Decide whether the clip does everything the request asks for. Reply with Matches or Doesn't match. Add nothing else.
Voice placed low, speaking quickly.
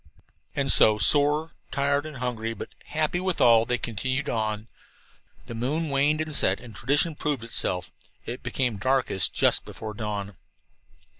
Doesn't match